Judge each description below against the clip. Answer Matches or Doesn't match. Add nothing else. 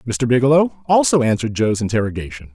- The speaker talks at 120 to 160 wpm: Matches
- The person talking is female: Doesn't match